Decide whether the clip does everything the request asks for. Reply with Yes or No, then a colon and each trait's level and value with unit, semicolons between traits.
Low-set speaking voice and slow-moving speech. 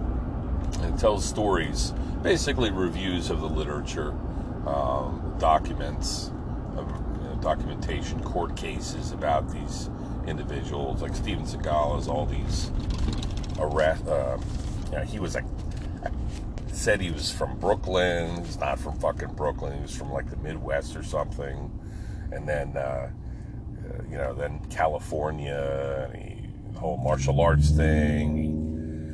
Yes: very low, 80 Hz; slow, 130 wpm